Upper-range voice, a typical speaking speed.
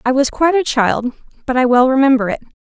No: very high, 260 Hz; fast, 230 wpm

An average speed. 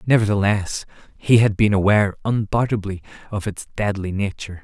No: slow, 130 wpm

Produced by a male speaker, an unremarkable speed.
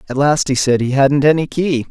No: male; fast, 250 wpm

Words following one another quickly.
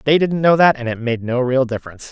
Yes: fast, 315 wpm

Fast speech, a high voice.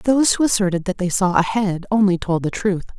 Yes: fast, 240 wpm; high, 195 Hz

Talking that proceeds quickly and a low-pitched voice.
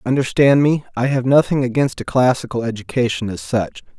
No: average, 150 wpm; low, 125 Hz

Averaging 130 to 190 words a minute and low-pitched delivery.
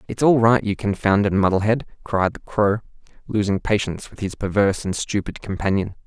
Yes: average, 170 wpm; low, 105 Hz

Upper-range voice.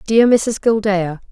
Yes: high, 210 Hz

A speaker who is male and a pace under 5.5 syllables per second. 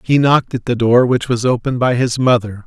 No: male; 5.8 syllables/s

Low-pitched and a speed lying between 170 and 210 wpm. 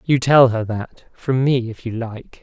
Yes: low, 120 Hz; average, 200 wpm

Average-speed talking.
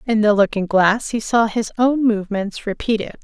Yes: average, 185 wpm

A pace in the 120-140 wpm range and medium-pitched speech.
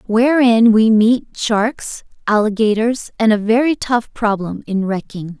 No: slow, 135 wpm; high, 220 Hz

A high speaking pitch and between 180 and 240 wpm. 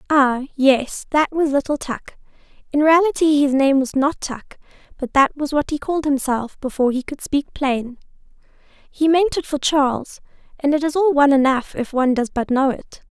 Yes: very high, 280 Hz; average, 190 wpm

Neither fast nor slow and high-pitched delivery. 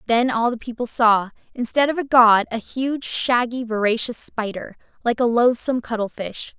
Yes: average, 165 wpm; high, 235 Hz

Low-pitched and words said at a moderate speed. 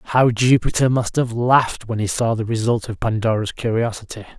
Yes: low, 115 Hz; average, 180 wpm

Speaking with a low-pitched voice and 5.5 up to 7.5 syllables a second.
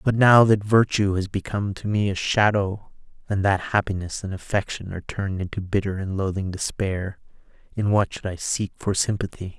No: low, 100 Hz; 5.2 syllables/s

